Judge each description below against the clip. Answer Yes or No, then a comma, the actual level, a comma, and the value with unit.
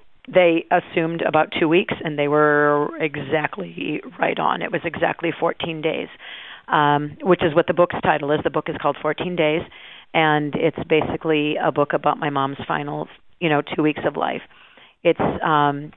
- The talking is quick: No, average, 175 wpm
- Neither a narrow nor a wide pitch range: No, narrow, 2.2 semitones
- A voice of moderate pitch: Yes, medium, 155 Hz